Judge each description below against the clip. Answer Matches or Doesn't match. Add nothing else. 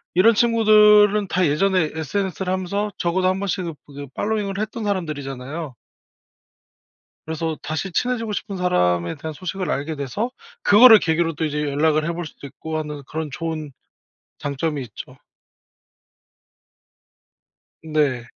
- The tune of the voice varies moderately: Matches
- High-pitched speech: Doesn't match